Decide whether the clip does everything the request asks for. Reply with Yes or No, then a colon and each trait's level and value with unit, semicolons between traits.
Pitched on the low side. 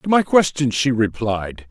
Yes: low, 125 Hz